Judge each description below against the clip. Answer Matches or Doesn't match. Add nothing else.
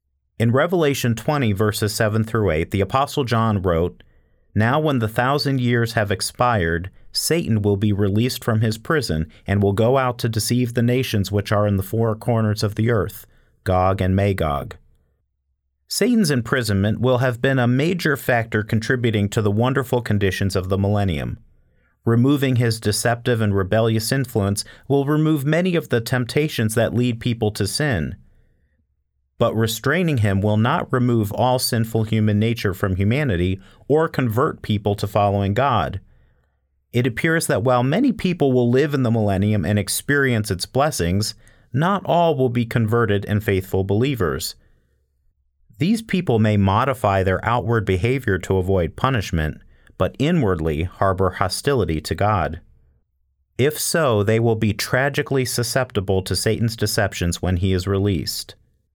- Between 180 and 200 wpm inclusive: Doesn't match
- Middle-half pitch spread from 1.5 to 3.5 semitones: Doesn't match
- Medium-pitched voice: Doesn't match